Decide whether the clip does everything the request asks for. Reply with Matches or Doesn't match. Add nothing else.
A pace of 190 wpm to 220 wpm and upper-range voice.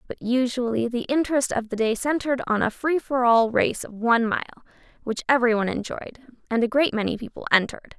Matches